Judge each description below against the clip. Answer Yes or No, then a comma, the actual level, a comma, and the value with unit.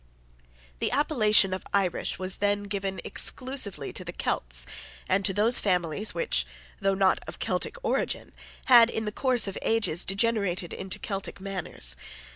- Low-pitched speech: No, high, 200 Hz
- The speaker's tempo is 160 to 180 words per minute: No, average, 150 wpm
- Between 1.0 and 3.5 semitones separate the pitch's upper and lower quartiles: Yes, average, 2.9 semitones